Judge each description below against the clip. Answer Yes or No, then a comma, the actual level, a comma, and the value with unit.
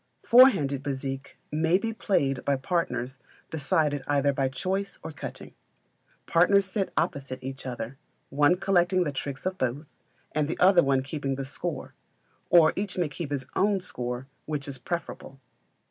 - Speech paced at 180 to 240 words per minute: No, average, 155 wpm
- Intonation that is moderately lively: Yes, average, 4.8 semitones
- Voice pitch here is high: No, medium, 145 Hz